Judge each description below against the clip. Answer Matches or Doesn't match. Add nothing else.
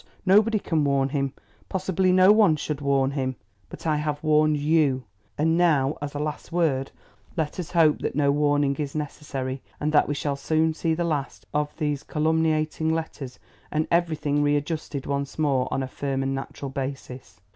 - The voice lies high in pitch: Doesn't match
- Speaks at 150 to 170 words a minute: Doesn't match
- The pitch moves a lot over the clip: Doesn't match